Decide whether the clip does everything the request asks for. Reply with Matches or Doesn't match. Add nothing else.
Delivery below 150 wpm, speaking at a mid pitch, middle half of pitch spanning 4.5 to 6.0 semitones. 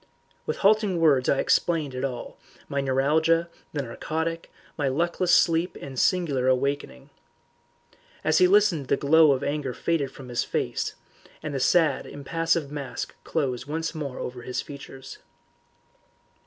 Doesn't match